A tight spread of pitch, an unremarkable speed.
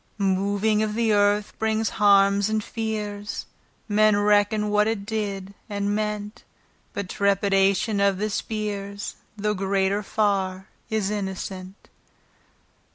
No: narrow, 1.1 semitones; slow, 115 wpm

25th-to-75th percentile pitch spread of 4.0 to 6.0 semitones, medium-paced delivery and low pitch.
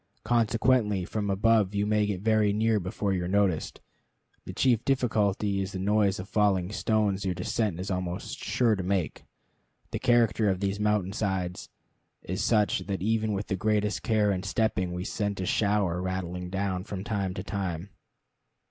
No: narrow, 2.4 semitones; average, 175 wpm; low, 100 Hz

